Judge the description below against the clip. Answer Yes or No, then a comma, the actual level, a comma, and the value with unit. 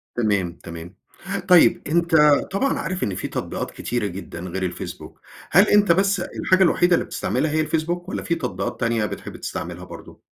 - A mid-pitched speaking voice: Yes, medium, 155 Hz